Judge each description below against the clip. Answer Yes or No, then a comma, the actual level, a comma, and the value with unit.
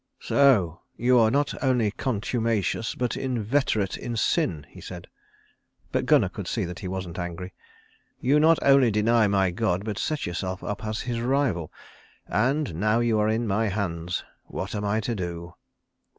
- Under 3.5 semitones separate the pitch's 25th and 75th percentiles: No, average, 4.7 semitones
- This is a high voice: No, low, 110 Hz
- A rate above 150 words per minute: Yes, average, 165 wpm